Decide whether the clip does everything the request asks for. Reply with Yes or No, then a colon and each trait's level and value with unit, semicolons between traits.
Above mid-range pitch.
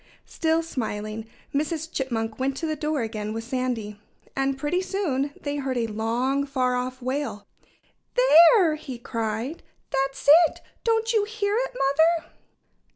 Yes: very high, 270 Hz